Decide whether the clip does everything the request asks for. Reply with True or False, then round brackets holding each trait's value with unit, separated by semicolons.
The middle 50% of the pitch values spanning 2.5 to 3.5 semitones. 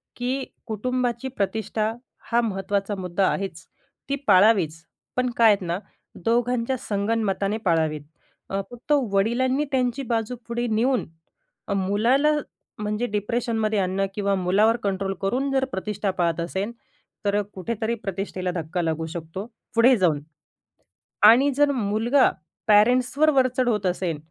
False (4.1 semitones)